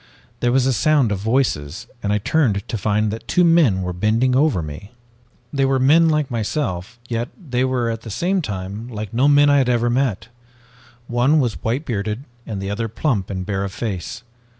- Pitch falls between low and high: No, low, 115 Hz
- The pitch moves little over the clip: No, average, 4.7 semitones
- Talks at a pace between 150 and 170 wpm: No, average, 200 wpm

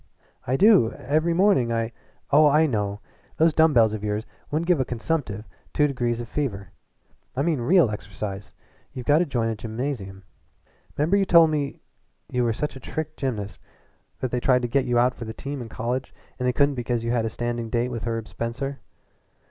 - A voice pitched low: Yes, low, 125 Hz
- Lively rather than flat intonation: No, average, 4.4 semitones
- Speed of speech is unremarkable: No, fast, 210 wpm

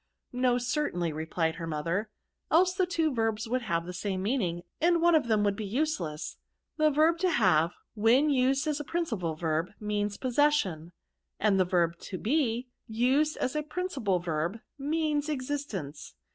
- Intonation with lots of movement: Yes, wide, 8.8 semitones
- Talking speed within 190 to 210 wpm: No, average, 175 wpm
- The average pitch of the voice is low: No, high, 225 Hz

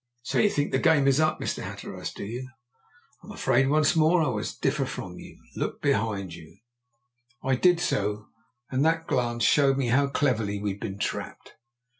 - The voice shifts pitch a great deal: Yes, wide, 6.0 semitones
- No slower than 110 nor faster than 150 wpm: No, average, 180 wpm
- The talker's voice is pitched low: Yes, low, 130 Hz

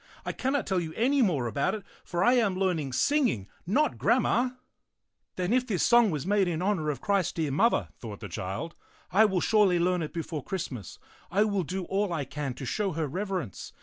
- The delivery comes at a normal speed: No, fast, 215 wpm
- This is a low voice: No, medium, 185 Hz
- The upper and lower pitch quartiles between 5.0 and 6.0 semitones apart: Yes, wide, 5.4 semitones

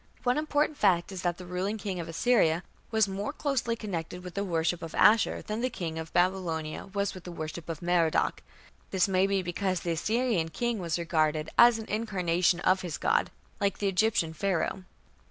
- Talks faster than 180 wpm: Yes, average, 190 wpm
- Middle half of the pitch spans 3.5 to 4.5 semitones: Yes, average, 3.9 semitones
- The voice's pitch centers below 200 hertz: Yes, medium, 185 Hz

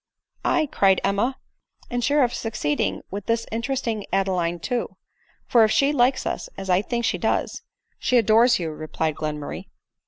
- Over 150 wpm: Yes, average, 180 wpm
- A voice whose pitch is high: Yes, high, 220 Hz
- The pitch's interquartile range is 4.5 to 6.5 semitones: Yes, average, 4.9 semitones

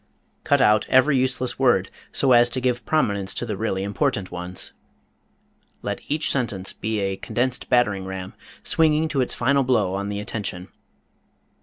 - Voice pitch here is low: Yes, low, 115 Hz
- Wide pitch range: No, average, 5.0 semitones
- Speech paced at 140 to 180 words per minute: Yes, average, 160 wpm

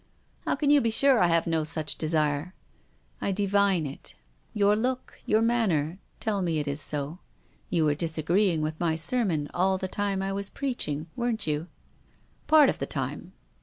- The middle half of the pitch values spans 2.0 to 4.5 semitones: No, average, 5.2 semitones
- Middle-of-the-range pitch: Yes, medium, 180 Hz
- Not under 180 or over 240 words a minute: Yes, average, 200 wpm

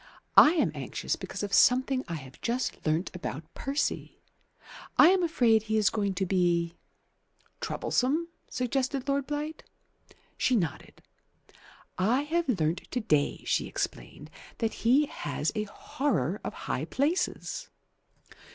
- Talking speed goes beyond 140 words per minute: No, slow, 135 wpm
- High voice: Yes, high, 235 Hz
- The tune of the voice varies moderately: No, wide, 7.4 semitones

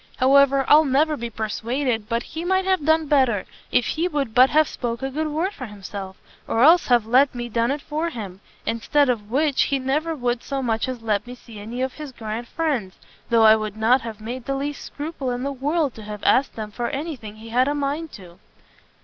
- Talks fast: Yes, fast, 225 wpm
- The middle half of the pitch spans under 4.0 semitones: No, average, 4.5 semitones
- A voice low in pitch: No, very high, 255 Hz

